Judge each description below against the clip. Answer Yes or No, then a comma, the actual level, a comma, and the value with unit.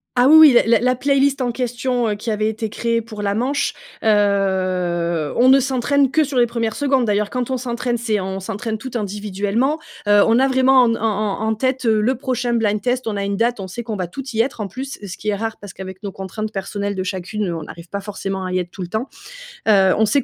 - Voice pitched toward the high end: Yes, high, 220 Hz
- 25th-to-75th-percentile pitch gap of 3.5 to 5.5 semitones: Yes, average, 3.9 semitones